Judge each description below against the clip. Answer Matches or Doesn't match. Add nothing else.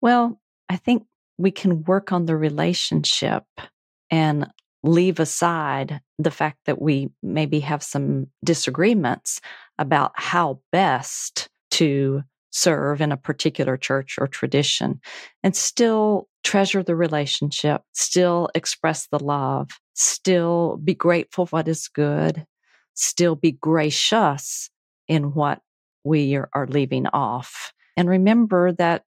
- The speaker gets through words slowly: Matches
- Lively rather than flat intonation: Doesn't match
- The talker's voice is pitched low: Doesn't match